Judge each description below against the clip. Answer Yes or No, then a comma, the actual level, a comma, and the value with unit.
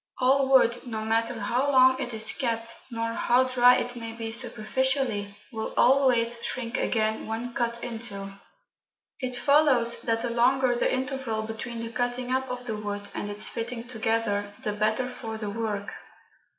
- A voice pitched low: No, high, 235 Hz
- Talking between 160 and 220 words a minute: Yes, average, 165 wpm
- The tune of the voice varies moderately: No, narrow, 2.3 semitones